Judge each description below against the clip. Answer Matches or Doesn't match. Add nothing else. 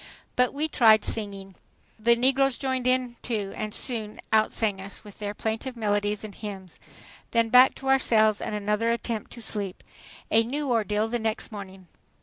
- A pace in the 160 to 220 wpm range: Matches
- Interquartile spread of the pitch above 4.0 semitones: Doesn't match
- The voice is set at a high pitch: Matches